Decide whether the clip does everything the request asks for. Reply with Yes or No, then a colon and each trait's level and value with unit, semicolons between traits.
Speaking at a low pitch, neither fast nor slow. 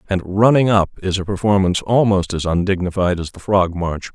Yes: very low, 95 Hz; average, 190 wpm